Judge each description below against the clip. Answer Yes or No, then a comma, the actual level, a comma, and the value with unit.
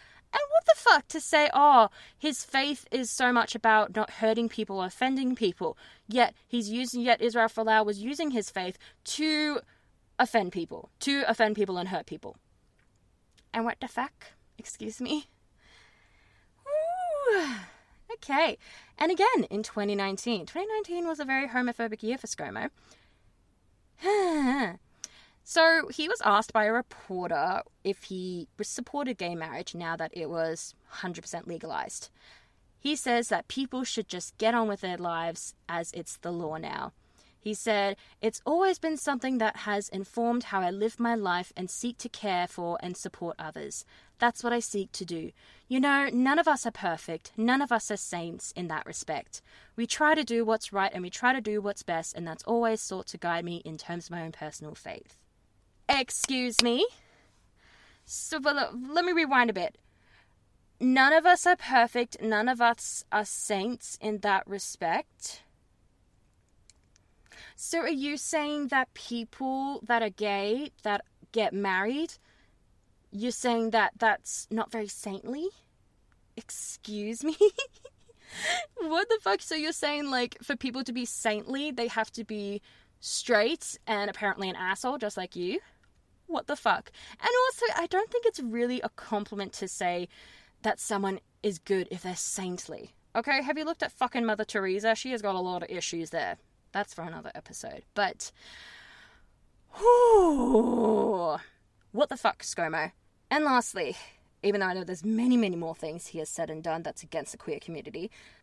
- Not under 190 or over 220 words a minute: No, average, 165 wpm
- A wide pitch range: Yes, wide, 6.3 semitones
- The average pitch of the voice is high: Yes, high, 230 Hz